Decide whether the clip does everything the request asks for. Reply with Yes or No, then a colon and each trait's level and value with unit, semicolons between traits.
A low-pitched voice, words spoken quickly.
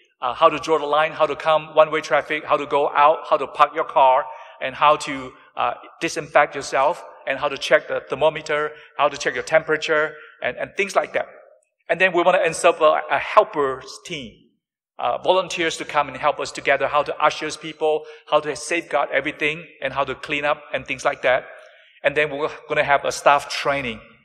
No: medium, 155 Hz; fast, 215 wpm